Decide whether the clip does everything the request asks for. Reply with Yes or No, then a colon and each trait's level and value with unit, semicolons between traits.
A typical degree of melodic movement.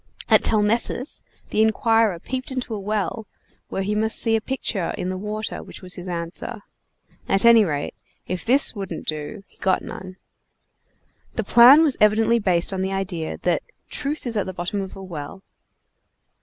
Yes: average, 3.4 semitones